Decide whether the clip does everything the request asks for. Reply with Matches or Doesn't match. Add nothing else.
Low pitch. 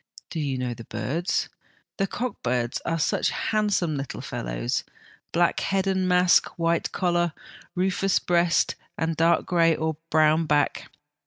Doesn't match